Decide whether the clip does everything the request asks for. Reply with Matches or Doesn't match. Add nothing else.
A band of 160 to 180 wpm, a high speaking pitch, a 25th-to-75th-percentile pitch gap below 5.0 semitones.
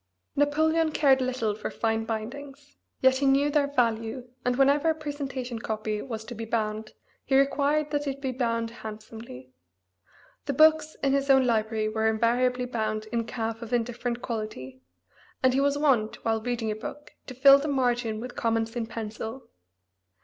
Matches